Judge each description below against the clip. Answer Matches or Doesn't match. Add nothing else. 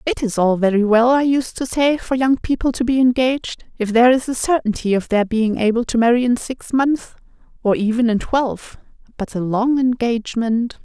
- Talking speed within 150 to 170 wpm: Doesn't match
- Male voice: Doesn't match